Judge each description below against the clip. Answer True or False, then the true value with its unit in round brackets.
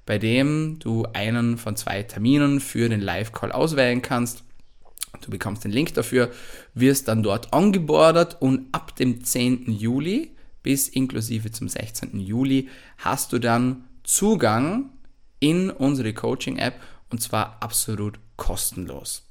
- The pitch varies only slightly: False (3.3 semitones)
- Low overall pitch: True (125 Hz)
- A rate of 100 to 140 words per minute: True (130 wpm)